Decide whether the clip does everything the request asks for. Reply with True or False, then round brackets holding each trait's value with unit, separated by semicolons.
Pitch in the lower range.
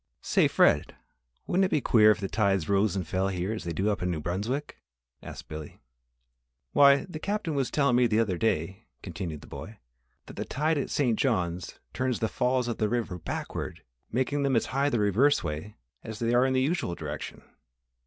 True (110 Hz)